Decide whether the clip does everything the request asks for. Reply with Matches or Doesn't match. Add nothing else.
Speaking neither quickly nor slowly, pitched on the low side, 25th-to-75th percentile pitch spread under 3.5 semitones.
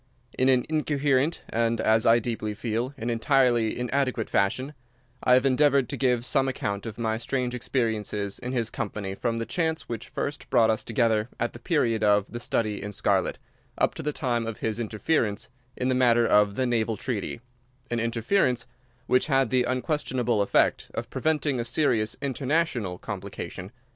Matches